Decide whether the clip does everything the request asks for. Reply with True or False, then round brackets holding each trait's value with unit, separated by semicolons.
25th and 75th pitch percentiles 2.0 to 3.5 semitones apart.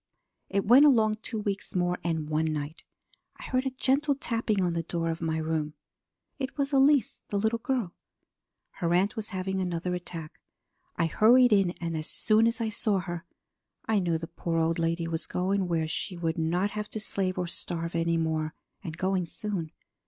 False (4.7 semitones)